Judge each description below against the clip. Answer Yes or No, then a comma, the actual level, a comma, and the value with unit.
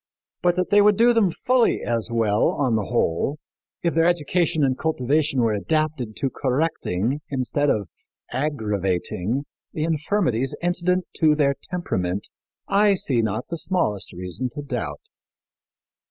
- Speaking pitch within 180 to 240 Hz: No, medium, 140 Hz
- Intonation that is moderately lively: No, wide, 7.2 semitones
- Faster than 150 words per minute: No, average, 140 wpm